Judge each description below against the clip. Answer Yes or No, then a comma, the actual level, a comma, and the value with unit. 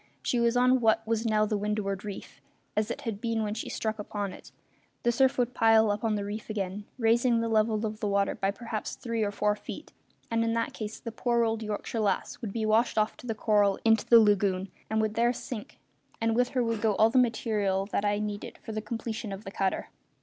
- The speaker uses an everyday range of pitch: No, narrow, 1.7 semitones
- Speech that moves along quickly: Yes, fast, 230 wpm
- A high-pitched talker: Yes, high, 220 Hz